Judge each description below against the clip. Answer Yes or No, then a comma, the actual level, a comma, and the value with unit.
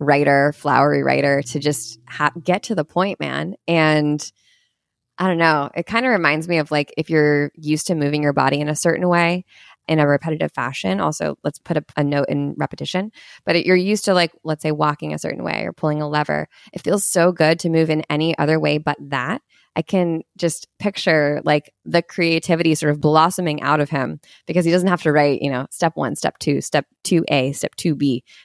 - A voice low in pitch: No, medium, 155 Hz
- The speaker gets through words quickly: Yes, fast, 215 wpm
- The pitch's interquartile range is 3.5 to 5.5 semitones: No, average, 2.8 semitones